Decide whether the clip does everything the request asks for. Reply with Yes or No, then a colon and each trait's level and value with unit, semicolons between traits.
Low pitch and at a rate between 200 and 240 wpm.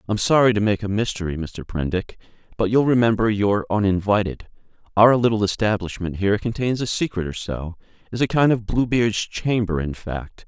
No: low, 105 Hz; average, 180 wpm